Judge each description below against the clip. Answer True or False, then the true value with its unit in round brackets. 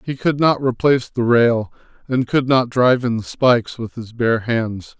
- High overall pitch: False (120 Hz)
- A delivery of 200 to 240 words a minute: True (205 wpm)